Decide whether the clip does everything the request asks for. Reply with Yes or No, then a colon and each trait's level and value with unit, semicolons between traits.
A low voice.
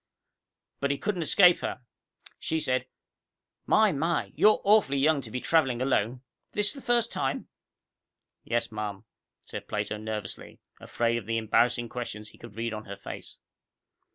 Yes: low, 125 Hz